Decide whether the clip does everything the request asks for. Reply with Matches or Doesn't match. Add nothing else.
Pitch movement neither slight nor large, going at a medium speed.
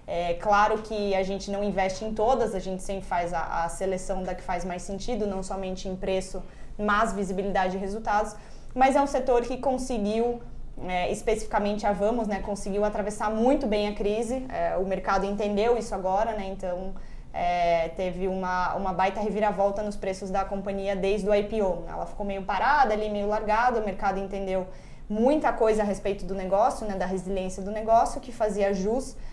Doesn't match